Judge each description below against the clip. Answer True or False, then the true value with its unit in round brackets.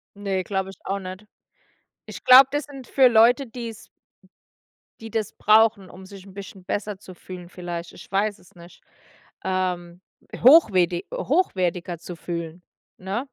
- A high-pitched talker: True (195 Hz)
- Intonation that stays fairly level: False (3.7 semitones)